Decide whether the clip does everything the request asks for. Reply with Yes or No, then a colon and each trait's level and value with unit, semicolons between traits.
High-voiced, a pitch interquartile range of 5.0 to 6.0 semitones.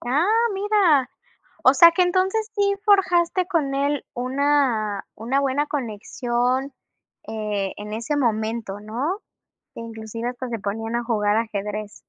Yes: very high, 250 Hz; wide, 5.4 semitones